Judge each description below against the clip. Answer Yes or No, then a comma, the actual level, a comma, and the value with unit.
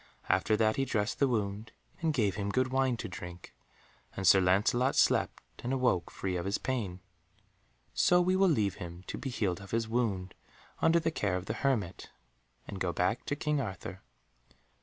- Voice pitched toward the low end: Yes, low, 105 Hz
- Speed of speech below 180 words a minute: No, average, 185 wpm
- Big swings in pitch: Yes, wide, 5.8 semitones